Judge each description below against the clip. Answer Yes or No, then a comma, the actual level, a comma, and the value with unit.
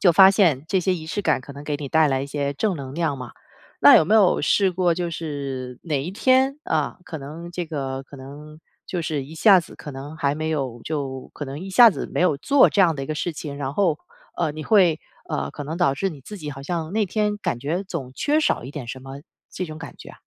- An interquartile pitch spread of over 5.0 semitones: No, average, 4.5 semitones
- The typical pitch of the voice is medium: Yes, medium, 155 Hz